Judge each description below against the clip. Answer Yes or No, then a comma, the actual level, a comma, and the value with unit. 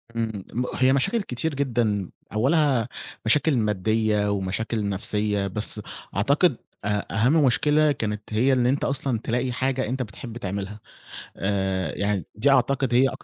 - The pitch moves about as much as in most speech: Yes, average, 4.4 semitones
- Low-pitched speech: Yes, low, 115 Hz